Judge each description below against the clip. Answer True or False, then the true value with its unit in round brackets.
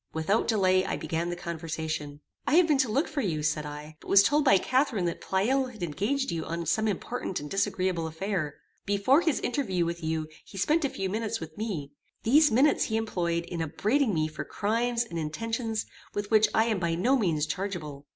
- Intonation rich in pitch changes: True (6.0 semitones)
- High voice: True (195 Hz)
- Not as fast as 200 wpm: False (205 wpm)